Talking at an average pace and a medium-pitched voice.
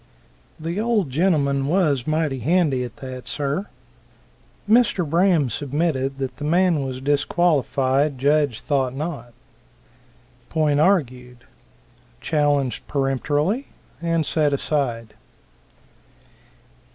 No: slow, 95 wpm; medium, 145 Hz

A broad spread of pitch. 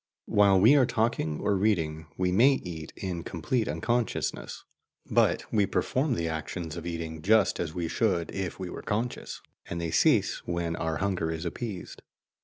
No: average, 4.7 semitones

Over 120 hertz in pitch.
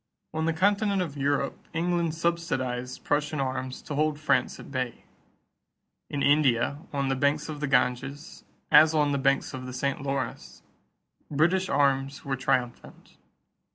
Yes: medium, 140 Hz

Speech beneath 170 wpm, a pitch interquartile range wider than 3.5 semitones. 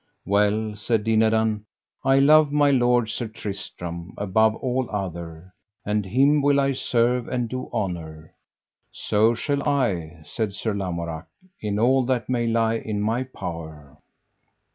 Yes: average, 140 wpm; average, 4.7 semitones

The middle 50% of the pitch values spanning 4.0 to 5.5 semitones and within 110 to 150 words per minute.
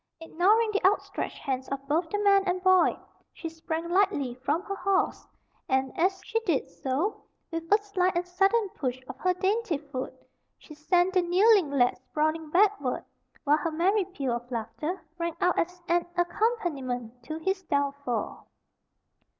No: average, 5.2 semitones; average, 160 wpm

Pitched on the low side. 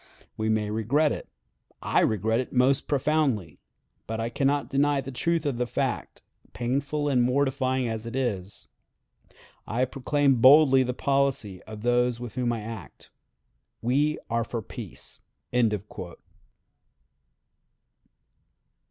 Yes: low, 125 Hz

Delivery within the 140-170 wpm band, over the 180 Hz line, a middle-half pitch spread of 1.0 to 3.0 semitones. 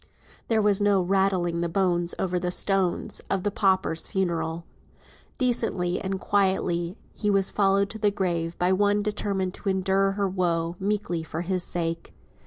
Yes: average, 160 wpm; high, 190 Hz; narrow, 2.4 semitones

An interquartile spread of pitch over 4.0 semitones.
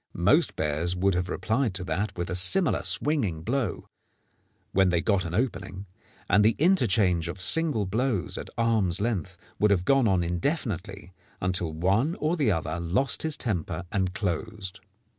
Yes: average, 4.5 semitones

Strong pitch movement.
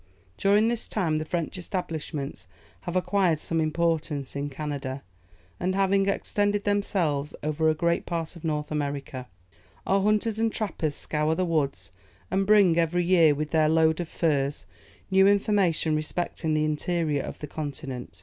No: average, 4.0 semitones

